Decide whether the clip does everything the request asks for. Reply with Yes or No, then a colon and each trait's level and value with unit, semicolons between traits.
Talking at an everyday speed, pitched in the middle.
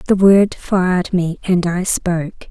Yes: average, 170 wpm; medium, 180 Hz